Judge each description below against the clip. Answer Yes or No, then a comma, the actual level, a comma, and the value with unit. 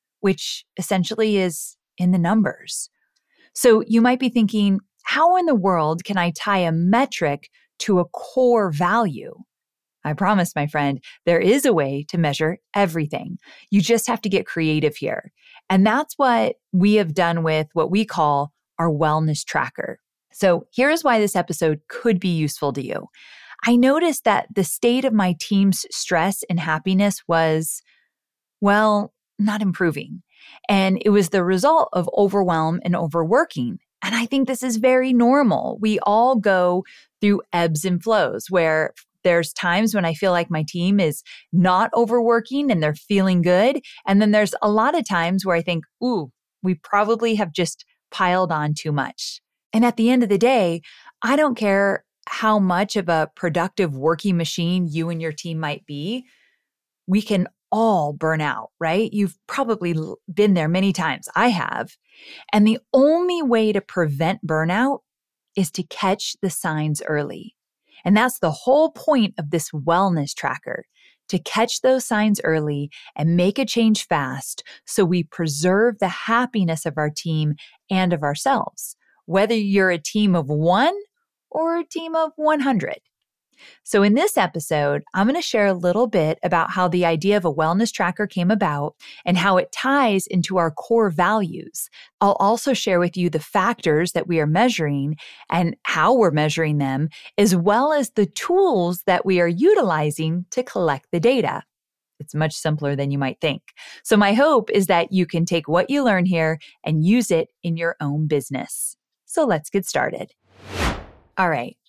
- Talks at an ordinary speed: Yes, average, 170 wpm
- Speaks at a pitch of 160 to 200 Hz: Yes, high, 190 Hz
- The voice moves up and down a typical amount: Yes, average, 5.0 semitones